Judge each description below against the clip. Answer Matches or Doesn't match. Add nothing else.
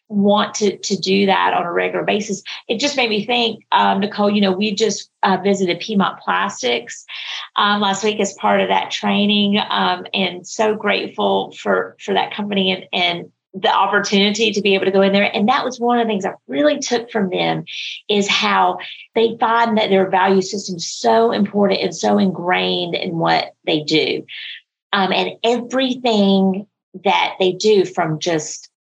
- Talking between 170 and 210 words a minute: Matches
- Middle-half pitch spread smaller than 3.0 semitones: Matches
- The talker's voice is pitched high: Matches